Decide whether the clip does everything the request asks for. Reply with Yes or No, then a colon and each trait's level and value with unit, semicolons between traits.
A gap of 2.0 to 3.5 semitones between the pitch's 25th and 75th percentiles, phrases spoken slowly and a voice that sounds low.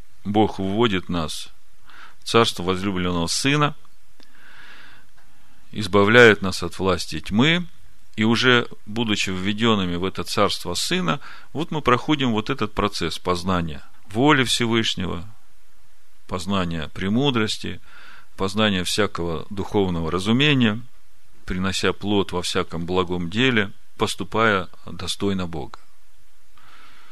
No: average, 4.1 semitones; slow, 95 wpm; low, 100 Hz